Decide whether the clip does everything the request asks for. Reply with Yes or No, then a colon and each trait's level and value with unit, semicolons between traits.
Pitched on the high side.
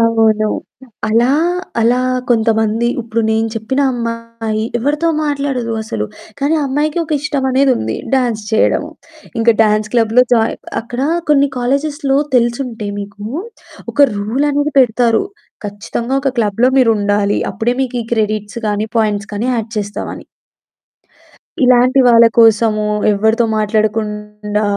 Yes: high, 230 Hz